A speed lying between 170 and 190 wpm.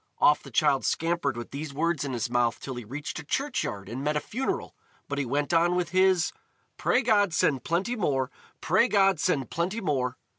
No: average, 200 wpm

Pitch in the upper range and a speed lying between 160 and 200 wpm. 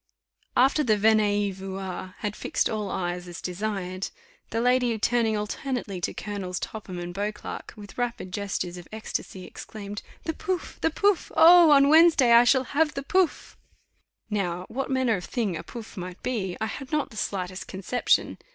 Yes: high, 215 Hz; average, 170 wpm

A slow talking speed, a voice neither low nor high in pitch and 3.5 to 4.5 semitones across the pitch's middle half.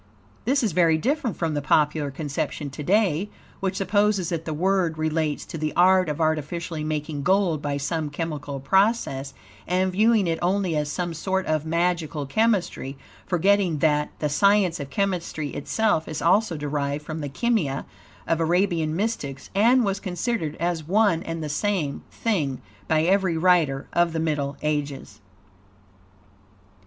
No: average, 155 wpm; medium, 165 Hz; average, 4.2 semitones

